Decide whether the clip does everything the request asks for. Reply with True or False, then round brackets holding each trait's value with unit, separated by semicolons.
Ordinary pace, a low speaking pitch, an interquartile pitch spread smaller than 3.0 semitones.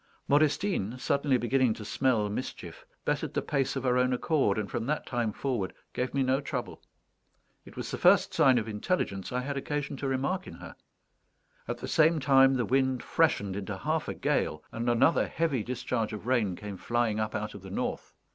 False (195 wpm; 125 Hz; 4.2 semitones)